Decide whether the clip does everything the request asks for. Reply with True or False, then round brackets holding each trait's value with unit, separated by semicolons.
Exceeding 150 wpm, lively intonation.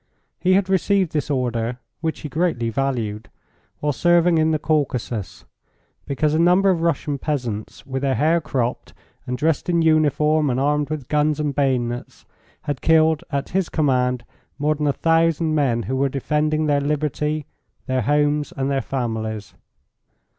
False (160 wpm; 3.3 semitones)